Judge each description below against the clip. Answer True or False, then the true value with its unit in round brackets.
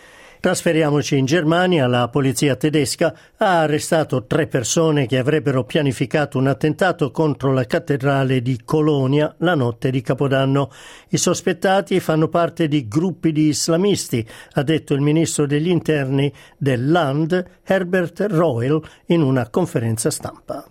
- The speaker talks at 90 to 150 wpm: True (130 wpm)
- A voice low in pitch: False (155 Hz)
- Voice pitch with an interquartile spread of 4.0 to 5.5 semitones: False (3.2 semitones)